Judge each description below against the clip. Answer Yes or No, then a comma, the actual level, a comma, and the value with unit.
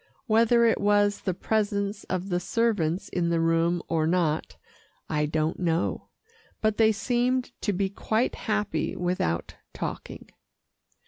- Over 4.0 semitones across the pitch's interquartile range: Yes, average, 4.5 semitones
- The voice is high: Yes, high, 195 Hz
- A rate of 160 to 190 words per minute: No, slow, 135 wpm